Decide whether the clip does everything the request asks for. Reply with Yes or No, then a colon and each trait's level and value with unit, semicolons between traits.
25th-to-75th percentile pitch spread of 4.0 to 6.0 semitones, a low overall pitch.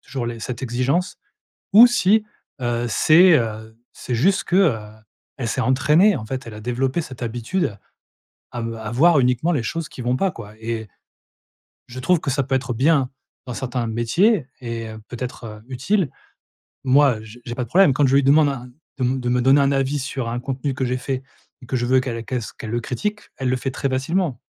No: average, 3.3 semitones; low, 130 Hz